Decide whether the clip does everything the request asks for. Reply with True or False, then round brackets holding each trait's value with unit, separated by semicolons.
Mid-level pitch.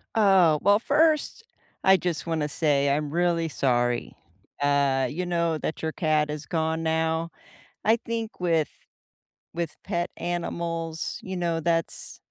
True (165 Hz)